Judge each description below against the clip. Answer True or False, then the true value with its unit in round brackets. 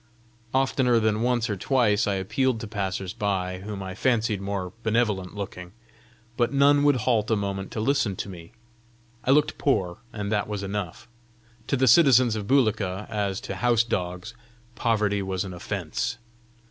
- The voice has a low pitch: True (105 Hz)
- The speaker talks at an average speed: True (165 wpm)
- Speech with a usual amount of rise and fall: True (3.7 semitones)